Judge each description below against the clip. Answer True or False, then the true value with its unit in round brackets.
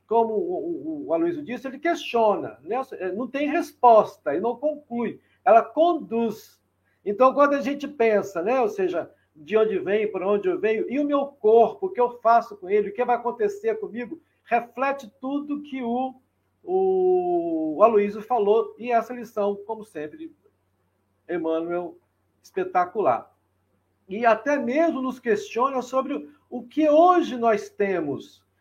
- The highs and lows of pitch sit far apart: True (6.0 semitones)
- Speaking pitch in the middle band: False (235 Hz)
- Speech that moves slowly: False (145 wpm)